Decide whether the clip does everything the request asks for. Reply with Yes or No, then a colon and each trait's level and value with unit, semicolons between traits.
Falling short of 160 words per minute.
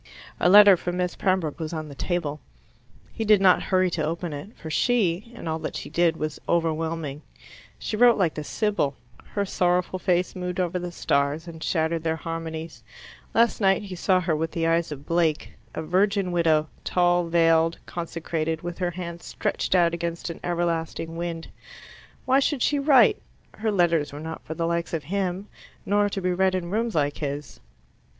No: average, 185 wpm